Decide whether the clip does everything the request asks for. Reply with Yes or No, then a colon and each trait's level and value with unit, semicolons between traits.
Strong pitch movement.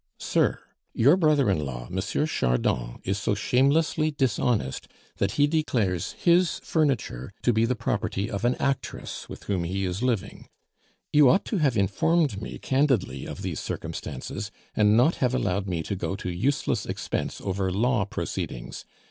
Yes: wide, 6.7 semitones